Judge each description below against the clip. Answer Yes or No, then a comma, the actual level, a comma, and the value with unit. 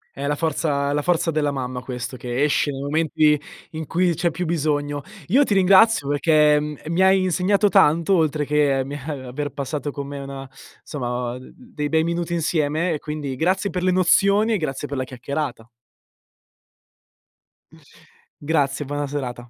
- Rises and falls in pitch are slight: No, average, 3.3 semitones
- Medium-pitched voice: Yes, medium, 150 Hz